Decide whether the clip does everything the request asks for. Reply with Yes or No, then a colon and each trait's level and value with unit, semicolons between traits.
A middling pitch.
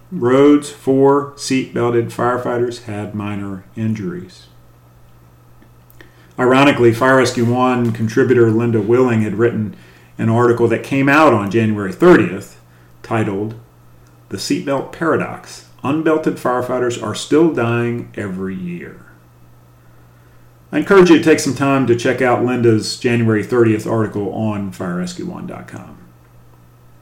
No: low, 115 Hz